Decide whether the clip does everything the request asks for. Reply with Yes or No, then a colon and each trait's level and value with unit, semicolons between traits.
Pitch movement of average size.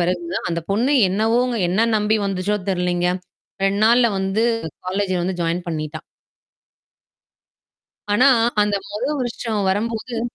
Yes: average, 4.1 semitones